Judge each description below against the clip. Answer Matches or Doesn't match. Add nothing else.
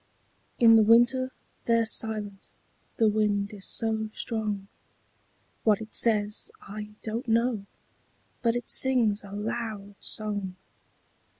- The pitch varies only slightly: Matches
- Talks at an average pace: Doesn't match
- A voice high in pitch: Matches